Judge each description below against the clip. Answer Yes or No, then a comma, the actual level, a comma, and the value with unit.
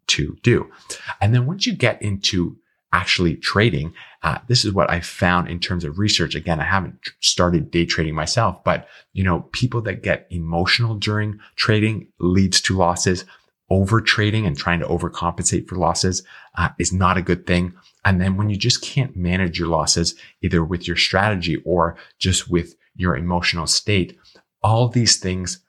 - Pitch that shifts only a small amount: No, average, 3.3 semitones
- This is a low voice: Yes, very low, 90 Hz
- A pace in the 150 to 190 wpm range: Yes, average, 175 wpm